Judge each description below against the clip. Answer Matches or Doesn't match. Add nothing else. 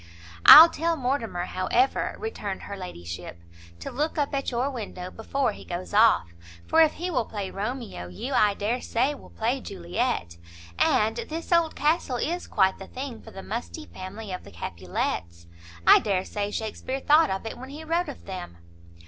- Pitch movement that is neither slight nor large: Doesn't match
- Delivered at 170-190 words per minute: Matches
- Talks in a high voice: Matches